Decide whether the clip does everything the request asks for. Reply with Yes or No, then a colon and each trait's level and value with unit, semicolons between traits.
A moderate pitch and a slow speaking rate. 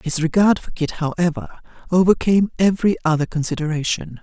Yes: medium, 170 Hz; slow, 130 wpm